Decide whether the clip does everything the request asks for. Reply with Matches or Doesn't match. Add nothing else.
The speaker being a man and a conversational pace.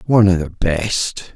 Matches